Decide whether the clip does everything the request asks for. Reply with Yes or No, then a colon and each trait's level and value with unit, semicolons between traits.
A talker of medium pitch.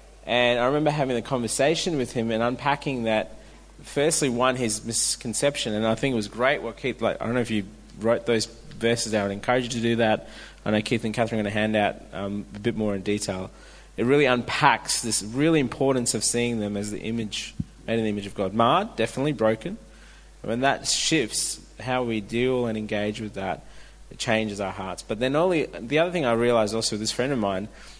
No: low, 115 Hz